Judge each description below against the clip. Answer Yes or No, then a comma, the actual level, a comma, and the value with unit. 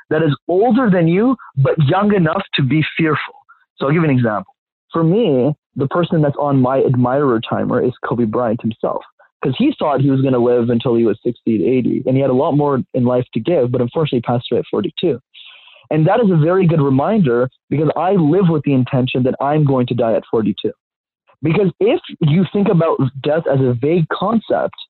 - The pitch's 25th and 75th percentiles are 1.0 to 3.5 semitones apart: No, average, 5.1 semitones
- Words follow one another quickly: Yes, fast, 220 wpm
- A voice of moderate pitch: Yes, medium, 145 Hz